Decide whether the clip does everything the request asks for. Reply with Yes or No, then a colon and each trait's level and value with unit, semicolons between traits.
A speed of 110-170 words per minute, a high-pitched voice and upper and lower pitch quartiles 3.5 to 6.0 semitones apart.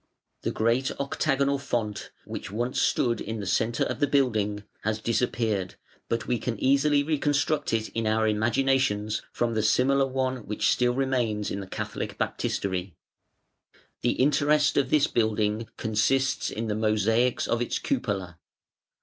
No: average, 150 wpm; low, 115 Hz; average, 3.9 semitones